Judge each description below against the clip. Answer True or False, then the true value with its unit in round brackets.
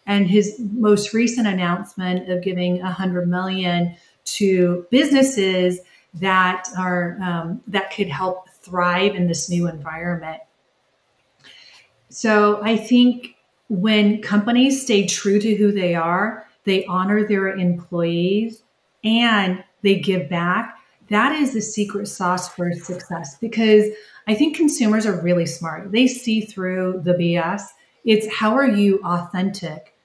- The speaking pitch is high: True (195 Hz)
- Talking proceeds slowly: True (130 wpm)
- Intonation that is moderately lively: True (3.2 semitones)